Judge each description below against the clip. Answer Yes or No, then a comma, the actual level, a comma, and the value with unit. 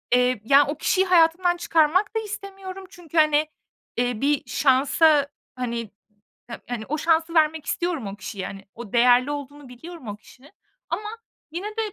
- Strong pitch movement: Yes, wide, 5.8 semitones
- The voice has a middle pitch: No, very high, 295 Hz